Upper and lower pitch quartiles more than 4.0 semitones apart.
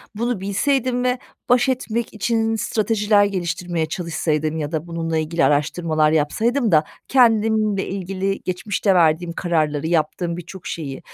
Yes: wide, 5.4 semitones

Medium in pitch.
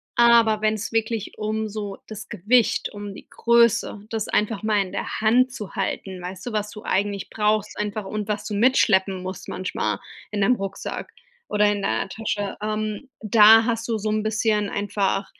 No: high, 210 Hz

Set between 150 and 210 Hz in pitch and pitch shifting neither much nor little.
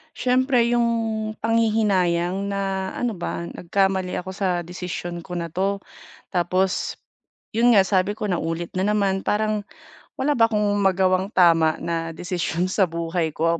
Yes: high, 190 Hz; average, 3.1 semitones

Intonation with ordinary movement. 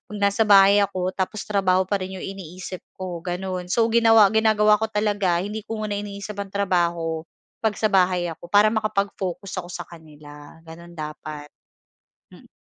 Yes: average, 3.1 semitones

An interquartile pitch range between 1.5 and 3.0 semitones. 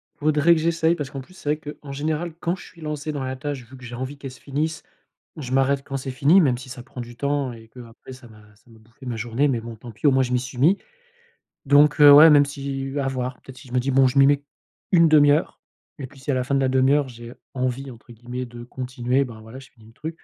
Yes: average, 2.7 semitones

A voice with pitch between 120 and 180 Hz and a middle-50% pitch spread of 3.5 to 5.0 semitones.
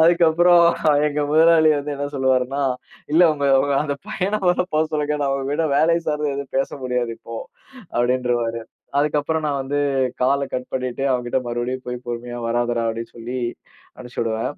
Yes: medium, 140 Hz; average, 3.8 semitones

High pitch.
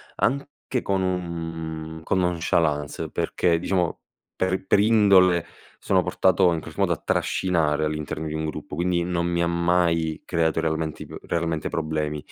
No: very low, 85 Hz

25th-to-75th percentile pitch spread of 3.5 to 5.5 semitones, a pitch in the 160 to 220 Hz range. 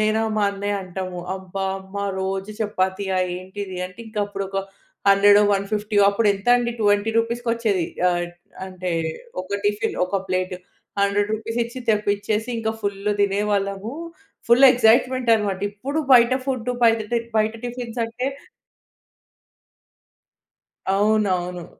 No: average, 2.7 semitones; high, 205 Hz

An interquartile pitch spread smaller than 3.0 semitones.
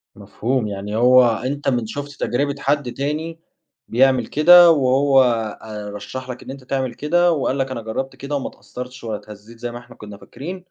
No: average, 3.4 semitones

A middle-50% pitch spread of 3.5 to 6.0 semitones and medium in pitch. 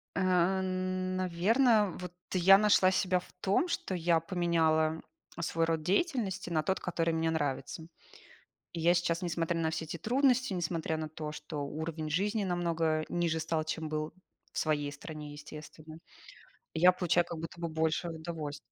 No: narrow, 2.6 semitones; medium, 165 Hz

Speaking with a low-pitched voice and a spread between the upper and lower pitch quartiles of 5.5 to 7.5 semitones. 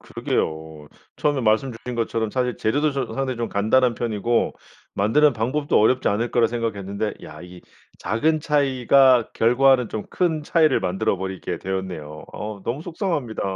No: low, 115 Hz; average, 5.1 semitones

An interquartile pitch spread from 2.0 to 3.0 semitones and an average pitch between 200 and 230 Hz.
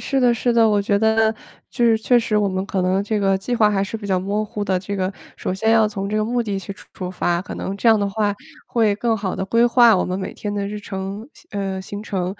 Yes: narrow, 2.4 semitones; high, 205 Hz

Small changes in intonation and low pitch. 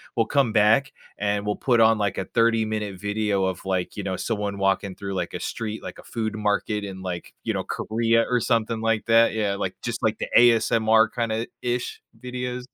Yes: narrow, 2.2 semitones; low, 110 Hz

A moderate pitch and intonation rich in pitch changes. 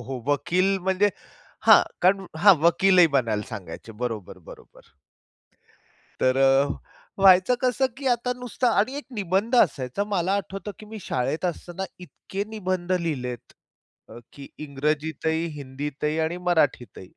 Yes: medium, 175 Hz; wide, 6.2 semitones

